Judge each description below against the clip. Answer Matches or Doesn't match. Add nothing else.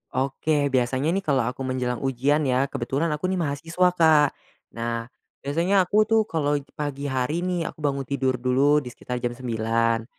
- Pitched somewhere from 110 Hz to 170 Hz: Matches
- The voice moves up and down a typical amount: Matches